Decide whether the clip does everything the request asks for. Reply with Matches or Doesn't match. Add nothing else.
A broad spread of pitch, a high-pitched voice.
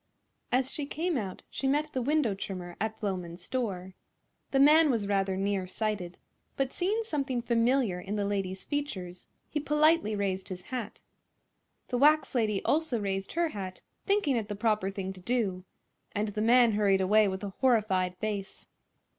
Matches